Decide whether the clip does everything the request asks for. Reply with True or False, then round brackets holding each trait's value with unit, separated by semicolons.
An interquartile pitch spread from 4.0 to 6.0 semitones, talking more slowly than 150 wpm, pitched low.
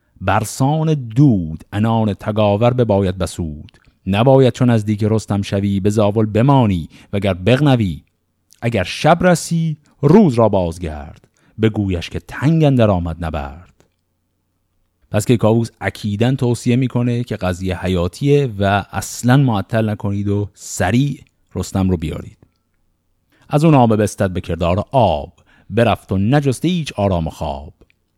True (5.2 semitones; 130 wpm; 105 Hz)